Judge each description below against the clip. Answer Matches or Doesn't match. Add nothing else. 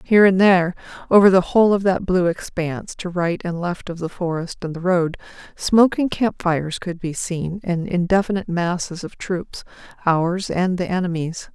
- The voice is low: Doesn't match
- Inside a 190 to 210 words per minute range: Doesn't match